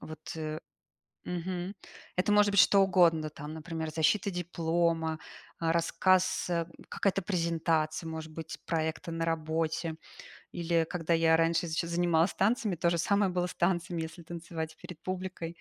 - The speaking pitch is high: No, medium, 170 Hz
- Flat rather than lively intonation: Yes, narrow, 1.7 semitones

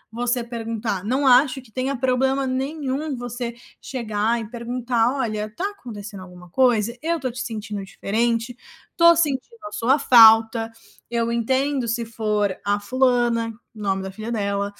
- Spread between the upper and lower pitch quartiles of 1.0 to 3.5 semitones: Yes, average, 3.1 semitones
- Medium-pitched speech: No, high, 235 Hz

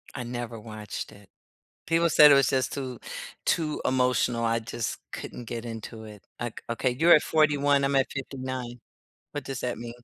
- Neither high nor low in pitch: No, low, 125 Hz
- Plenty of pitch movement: No, average, 3.1 semitones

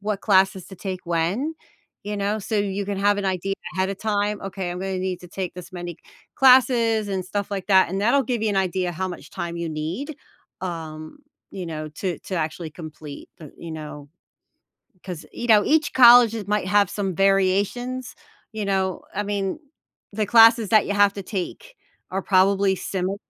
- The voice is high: Yes, high, 195 Hz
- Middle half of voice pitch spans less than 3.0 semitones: Yes, narrow, 2.5 semitones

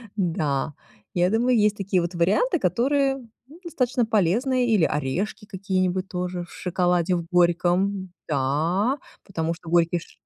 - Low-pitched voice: No, medium, 185 Hz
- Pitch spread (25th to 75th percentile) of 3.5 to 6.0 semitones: Yes, average, 4.2 semitones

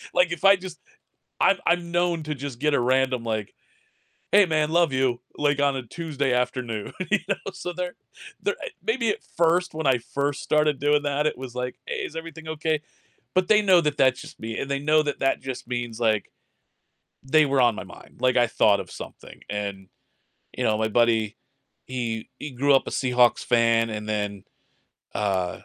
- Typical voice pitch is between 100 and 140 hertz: Yes, low, 135 Hz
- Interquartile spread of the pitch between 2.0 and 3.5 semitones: No, average, 5.0 semitones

